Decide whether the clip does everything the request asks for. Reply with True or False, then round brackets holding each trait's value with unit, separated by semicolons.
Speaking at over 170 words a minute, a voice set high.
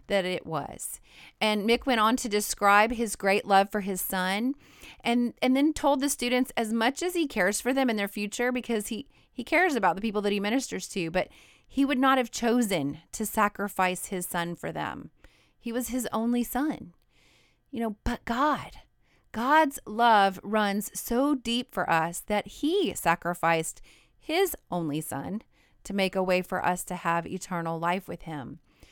True (185 wpm; 215 Hz)